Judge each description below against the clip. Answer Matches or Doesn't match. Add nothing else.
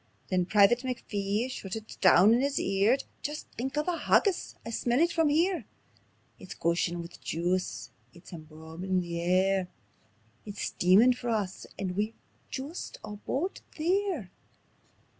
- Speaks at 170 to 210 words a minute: Doesn't match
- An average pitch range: Doesn't match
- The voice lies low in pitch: Doesn't match